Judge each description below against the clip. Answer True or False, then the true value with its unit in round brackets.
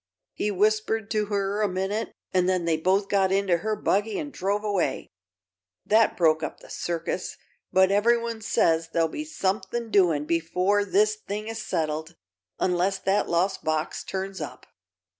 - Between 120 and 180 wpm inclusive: True (160 wpm)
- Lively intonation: False (3.5 semitones)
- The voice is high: True (195 Hz)